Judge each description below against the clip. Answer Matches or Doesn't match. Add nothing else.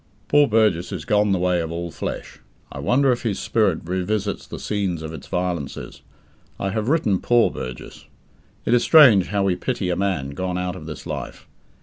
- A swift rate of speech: Doesn't match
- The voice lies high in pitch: Doesn't match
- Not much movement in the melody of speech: Doesn't match